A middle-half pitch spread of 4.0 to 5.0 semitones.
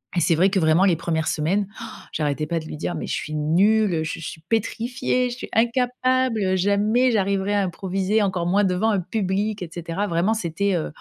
Yes: average, 4.5 semitones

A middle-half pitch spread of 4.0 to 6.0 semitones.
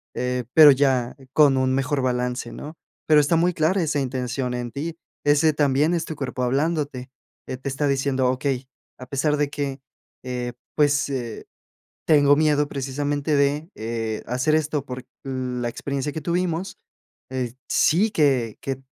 No: average, 2.8 semitones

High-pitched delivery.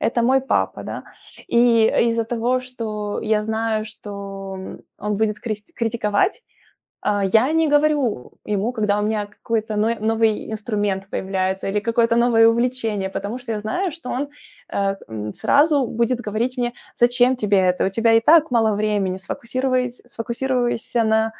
Yes: high, 225 Hz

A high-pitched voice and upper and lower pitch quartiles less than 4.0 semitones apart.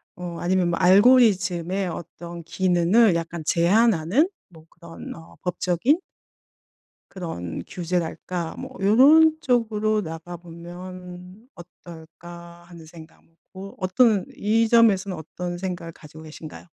No: medium, 180 Hz; average, 3.4 semitones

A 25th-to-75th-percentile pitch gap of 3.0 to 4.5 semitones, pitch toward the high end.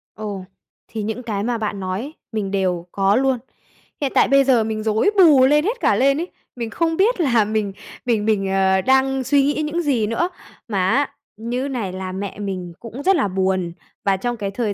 No: wide, 5.4 semitones; high, 225 Hz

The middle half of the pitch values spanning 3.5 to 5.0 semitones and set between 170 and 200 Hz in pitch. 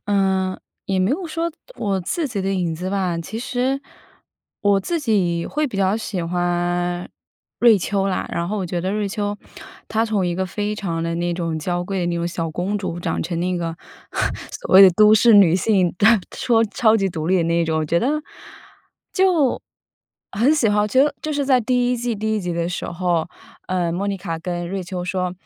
Yes: average, 3.8 semitones; high, 190 Hz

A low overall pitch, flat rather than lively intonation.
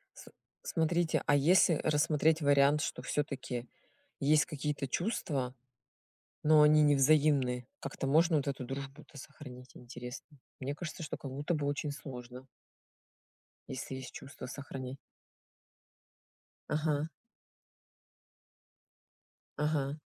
No: medium, 145 Hz; narrow, 2.3 semitones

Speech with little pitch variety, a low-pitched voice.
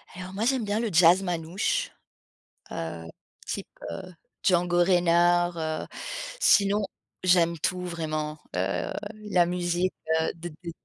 No: narrow, 2.0 semitones; medium, 175 Hz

